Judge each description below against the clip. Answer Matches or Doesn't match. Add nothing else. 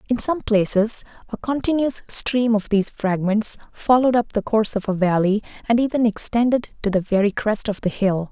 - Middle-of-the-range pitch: Doesn't match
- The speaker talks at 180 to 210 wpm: Matches